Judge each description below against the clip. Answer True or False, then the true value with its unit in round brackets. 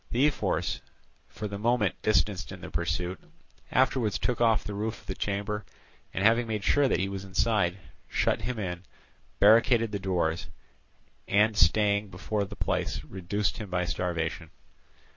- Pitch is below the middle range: True (100 Hz)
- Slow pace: False (160 wpm)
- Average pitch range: True (3.2 semitones)